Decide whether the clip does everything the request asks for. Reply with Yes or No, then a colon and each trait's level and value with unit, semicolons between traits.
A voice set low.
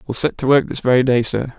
Yes: low, 125 Hz